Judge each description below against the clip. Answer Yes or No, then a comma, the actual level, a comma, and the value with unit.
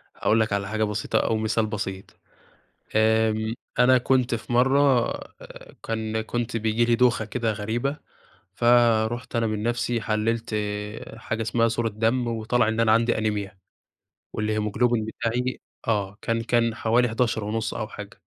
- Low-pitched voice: Yes, low, 115 Hz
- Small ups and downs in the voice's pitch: Yes, narrow, 1.6 semitones